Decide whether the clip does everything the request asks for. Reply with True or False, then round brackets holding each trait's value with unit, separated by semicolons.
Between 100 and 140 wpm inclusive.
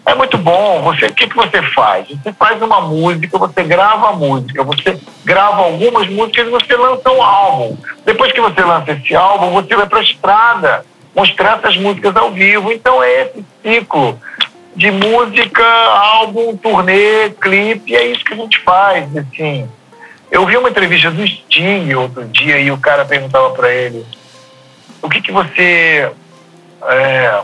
False (170 wpm)